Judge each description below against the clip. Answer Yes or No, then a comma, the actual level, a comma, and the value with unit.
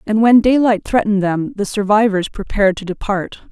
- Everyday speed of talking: Yes, average, 170 wpm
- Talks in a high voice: Yes, high, 210 Hz